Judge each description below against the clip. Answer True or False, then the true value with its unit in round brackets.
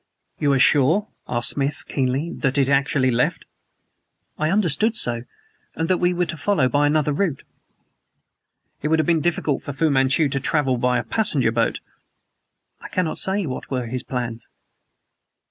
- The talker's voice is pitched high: False (145 Hz)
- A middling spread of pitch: True (4.1 semitones)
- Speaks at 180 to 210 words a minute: False (170 wpm)